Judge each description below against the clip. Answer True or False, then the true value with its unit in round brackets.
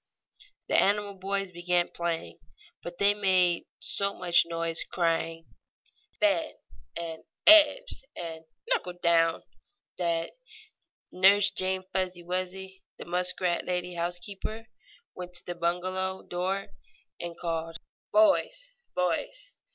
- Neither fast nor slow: False (110 wpm)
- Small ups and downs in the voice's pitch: True (2.3 semitones)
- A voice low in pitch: False (180 Hz)